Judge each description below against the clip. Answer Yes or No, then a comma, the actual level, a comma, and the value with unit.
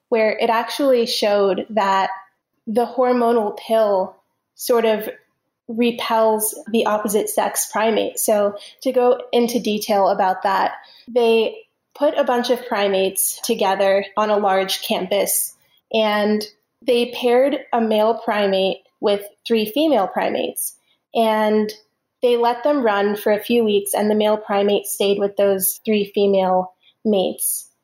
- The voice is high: Yes, high, 215 Hz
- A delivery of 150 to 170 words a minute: No, slow, 135 wpm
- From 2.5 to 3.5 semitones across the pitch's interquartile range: Yes, average, 2.8 semitones